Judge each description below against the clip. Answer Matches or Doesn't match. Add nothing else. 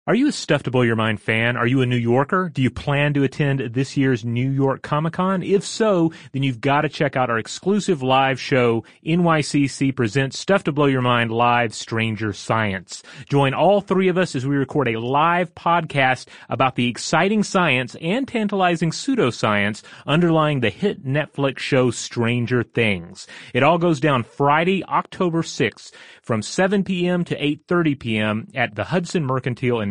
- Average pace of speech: Matches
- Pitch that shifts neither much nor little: Doesn't match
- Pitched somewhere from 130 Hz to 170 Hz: Matches